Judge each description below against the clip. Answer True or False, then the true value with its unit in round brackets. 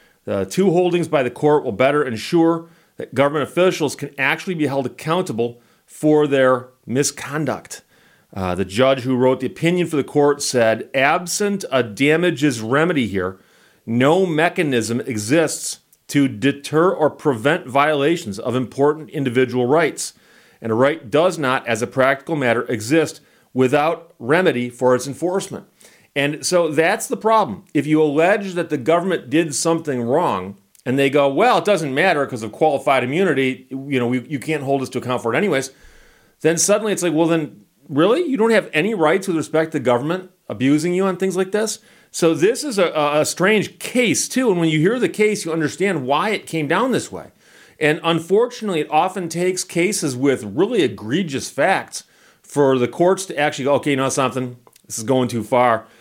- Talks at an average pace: True (180 wpm)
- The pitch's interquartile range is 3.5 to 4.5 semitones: False (5.0 semitones)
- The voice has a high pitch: False (150 Hz)